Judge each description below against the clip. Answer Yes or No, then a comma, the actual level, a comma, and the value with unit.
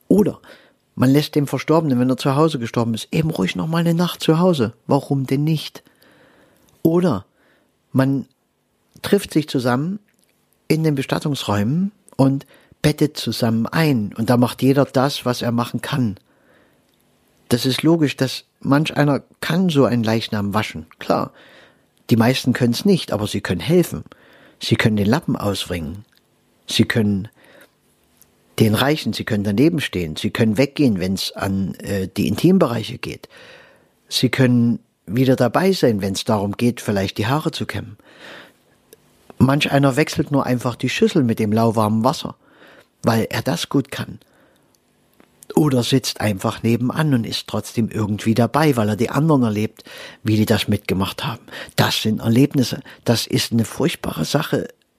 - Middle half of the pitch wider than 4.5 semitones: Yes, average, 4.9 semitones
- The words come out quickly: No, average, 155 wpm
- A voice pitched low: Yes, low, 125 Hz